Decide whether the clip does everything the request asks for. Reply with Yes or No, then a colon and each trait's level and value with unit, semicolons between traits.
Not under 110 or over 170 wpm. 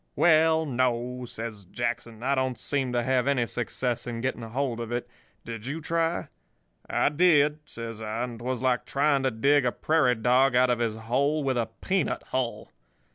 No: average, 185 wpm